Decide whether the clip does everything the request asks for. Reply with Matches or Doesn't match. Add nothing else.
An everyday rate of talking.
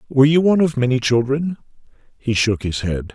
Matches